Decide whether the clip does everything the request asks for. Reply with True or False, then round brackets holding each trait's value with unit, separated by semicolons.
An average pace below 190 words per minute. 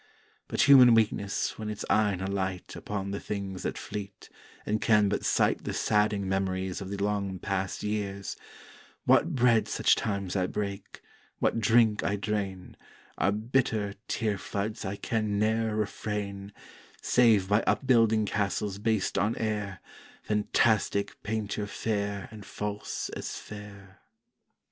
True (135 wpm)